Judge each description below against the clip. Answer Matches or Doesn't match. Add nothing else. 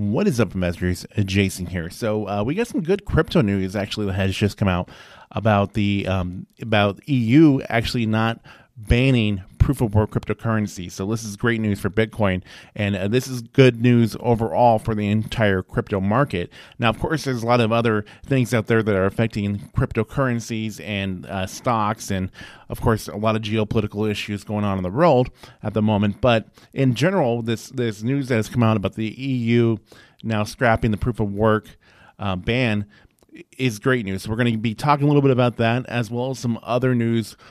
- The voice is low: Matches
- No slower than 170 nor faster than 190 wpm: Doesn't match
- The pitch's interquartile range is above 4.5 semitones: Doesn't match